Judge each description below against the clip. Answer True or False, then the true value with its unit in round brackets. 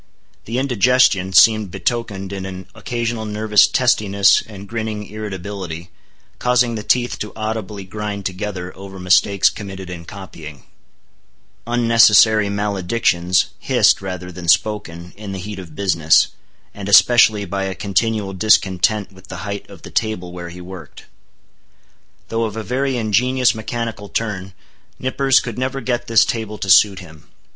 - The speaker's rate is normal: True (145 wpm)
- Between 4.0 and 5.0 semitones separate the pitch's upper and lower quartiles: False (3.1 semitones)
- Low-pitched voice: True (105 Hz)